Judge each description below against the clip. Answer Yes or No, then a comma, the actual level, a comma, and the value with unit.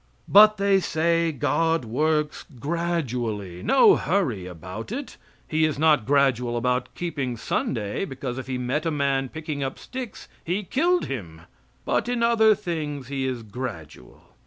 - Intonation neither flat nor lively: No, wide, 5.8 semitones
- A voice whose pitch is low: No, medium, 145 Hz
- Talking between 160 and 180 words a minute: No, average, 150 wpm